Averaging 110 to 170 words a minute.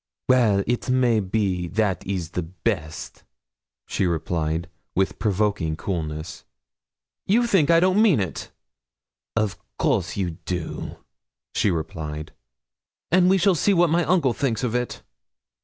Yes: slow, 135 wpm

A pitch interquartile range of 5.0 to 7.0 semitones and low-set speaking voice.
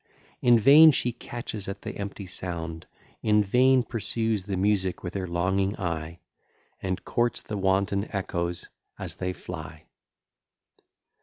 No: average, 3.4 semitones; low, 100 Hz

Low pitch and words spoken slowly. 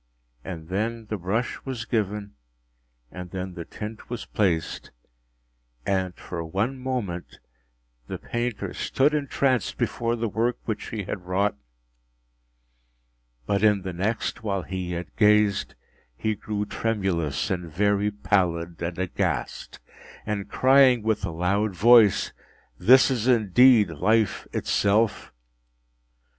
Yes: low, 105 Hz; slow, 125 wpm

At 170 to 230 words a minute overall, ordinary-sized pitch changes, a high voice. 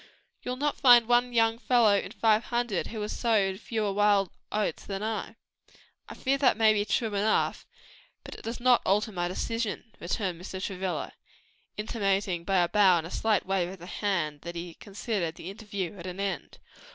Yes: average, 190 wpm; average, 3.2 semitones; high, 205 Hz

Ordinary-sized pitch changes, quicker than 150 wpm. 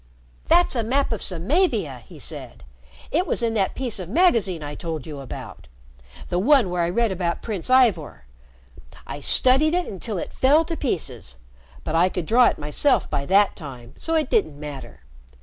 No: wide, 8.6 semitones; average, 185 wpm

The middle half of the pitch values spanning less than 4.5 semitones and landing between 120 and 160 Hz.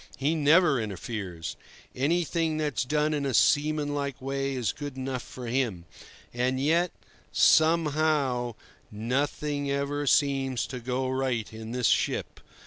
Yes: average, 3.1 semitones; low, 135 Hz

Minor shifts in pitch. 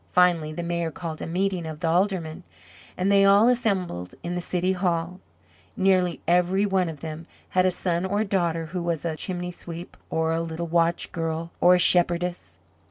Yes: narrow, 2.0 semitones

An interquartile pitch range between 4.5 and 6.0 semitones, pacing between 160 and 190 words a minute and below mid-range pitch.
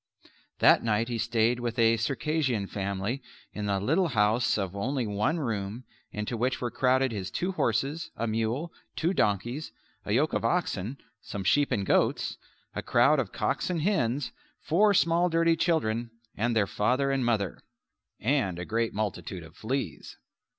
Yes: average, 5.3 semitones; average, 165 wpm; low, 120 Hz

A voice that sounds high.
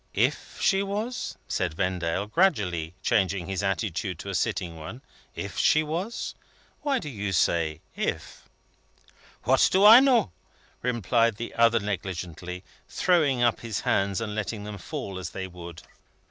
No: low, 105 Hz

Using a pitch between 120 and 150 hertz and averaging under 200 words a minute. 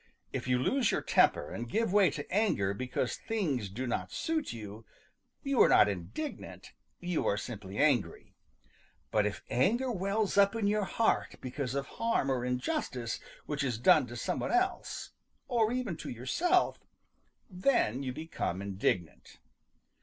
Yes: medium, 140 Hz; average, 155 wpm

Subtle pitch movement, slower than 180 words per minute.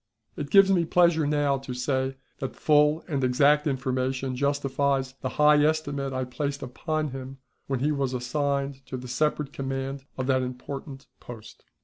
Yes: narrow, 2.3 semitones; average, 160 wpm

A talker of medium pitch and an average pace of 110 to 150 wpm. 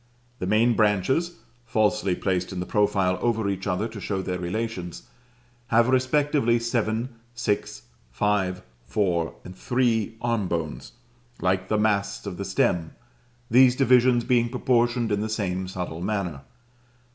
No: low, 105 Hz; average, 140 wpm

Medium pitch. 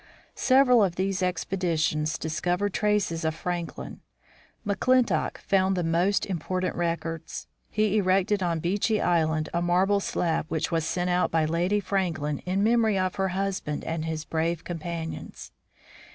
Yes: medium, 180 Hz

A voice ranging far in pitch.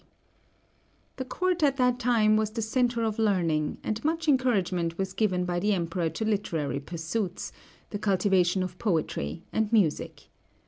No: average, 4.8 semitones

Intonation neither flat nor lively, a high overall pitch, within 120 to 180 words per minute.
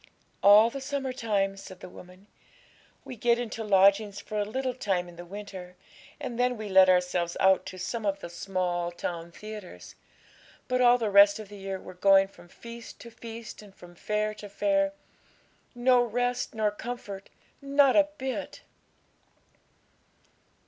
Yes: average, 4.2 semitones; high, 210 Hz; average, 165 wpm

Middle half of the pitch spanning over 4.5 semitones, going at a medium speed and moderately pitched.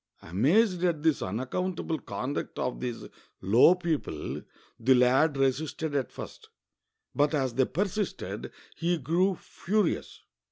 No: wide, 5.6 semitones; slow, 120 wpm; medium, 150 Hz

